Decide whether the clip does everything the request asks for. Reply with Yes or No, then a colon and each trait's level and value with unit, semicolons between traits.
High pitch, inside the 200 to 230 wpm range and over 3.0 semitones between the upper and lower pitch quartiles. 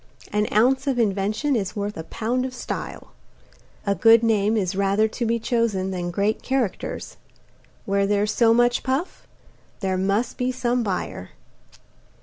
No: high, 215 Hz; average, 150 wpm; average, 3.4 semitones